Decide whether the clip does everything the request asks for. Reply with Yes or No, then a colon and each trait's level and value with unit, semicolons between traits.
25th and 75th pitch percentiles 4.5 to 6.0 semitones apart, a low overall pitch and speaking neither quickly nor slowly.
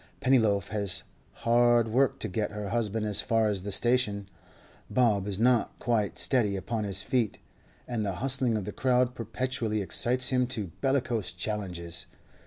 No: average, 3.4 semitones; low, 110 Hz; average, 160 wpm